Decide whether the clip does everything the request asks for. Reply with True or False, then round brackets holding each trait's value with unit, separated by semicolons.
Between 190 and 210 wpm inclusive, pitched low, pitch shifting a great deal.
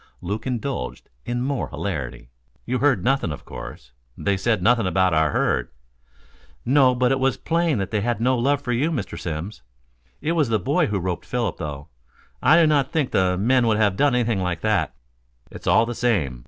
True (200 wpm; 115 Hz; 5.9 semitones)